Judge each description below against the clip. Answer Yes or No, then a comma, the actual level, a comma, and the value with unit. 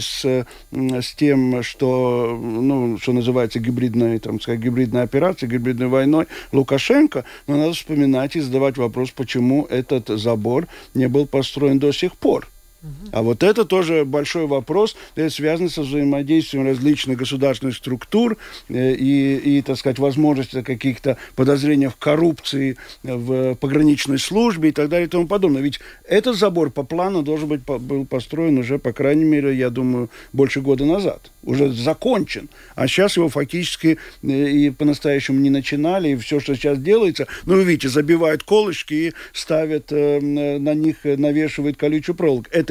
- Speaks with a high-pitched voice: No, medium, 140 Hz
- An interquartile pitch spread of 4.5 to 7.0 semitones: No, average, 3.0 semitones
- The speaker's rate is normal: Yes, average, 145 wpm